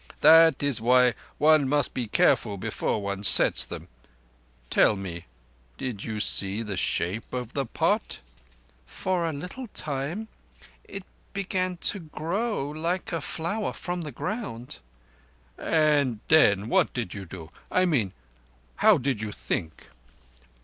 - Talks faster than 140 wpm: No, slow, 135 wpm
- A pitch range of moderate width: No, wide, 7.7 semitones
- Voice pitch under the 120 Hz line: No, medium, 140 Hz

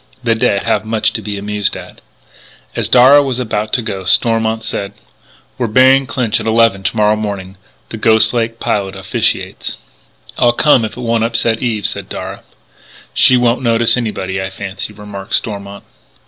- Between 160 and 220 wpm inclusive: Yes, average, 170 wpm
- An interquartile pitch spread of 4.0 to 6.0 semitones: No, narrow, 2.6 semitones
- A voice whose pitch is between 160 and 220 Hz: No, low, 110 Hz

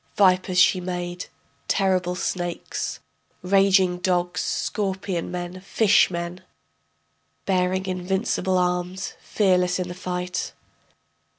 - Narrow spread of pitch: Yes, narrow, 1.1 semitones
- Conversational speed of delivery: No, slow, 95 wpm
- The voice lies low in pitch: No, medium, 180 Hz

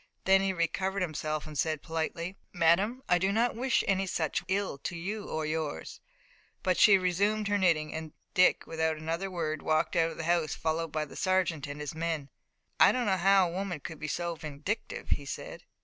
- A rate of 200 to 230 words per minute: Yes, fast, 205 wpm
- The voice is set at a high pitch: No, medium, 170 Hz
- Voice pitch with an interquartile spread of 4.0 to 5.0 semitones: No, average, 3.4 semitones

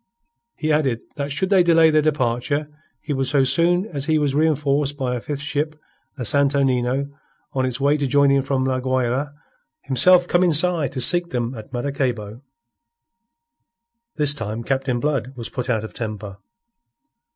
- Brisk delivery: No, average, 170 wpm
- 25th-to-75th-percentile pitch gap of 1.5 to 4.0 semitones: Yes, average, 3.2 semitones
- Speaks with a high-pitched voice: No, medium, 140 Hz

